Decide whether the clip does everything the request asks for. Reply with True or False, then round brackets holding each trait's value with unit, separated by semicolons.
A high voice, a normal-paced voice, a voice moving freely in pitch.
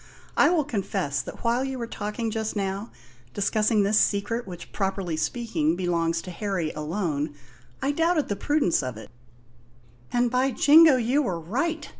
True (205 Hz; 165 wpm; 6.5 semitones)